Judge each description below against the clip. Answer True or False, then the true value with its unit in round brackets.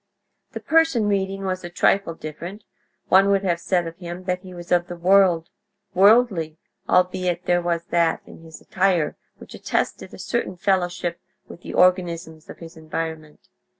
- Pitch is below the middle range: False (175 Hz)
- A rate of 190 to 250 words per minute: False (165 wpm)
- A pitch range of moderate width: False (2.2 semitones)